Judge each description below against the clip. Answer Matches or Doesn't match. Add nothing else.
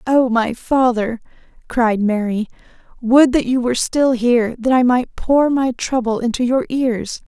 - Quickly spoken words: Doesn't match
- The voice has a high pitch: Matches